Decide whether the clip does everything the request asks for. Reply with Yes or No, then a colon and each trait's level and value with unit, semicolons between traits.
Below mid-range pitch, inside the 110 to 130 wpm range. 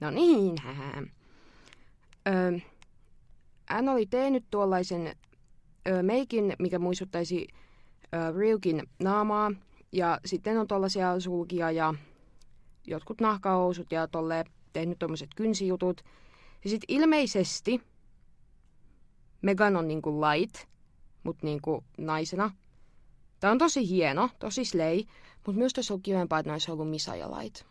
No: medium, 180 Hz; average, 115 wpm